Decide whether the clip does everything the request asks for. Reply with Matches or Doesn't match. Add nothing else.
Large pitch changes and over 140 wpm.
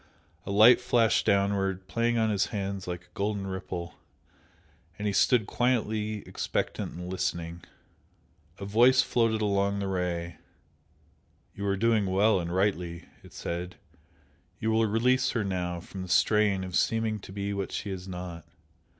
Doesn't match